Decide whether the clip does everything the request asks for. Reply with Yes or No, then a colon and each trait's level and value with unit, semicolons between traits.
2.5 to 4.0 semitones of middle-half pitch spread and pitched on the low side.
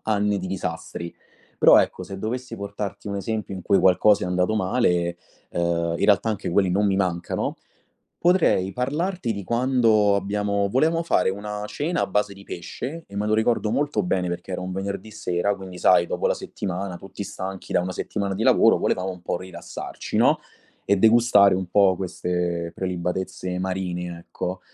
Yes: average, 2.8 semitones; low, 100 Hz